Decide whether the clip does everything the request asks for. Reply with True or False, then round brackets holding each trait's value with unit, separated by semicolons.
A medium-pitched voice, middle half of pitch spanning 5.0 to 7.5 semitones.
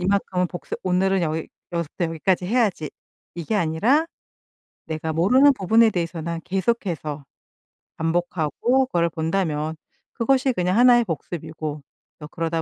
False (175 Hz; 4.6 semitones)